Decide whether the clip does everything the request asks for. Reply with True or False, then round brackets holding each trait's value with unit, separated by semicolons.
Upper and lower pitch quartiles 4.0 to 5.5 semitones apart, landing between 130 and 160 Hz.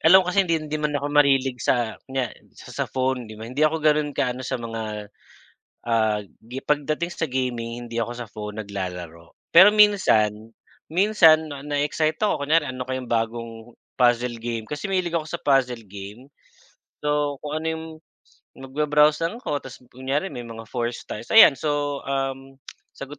True (4.5 semitones; 135 Hz)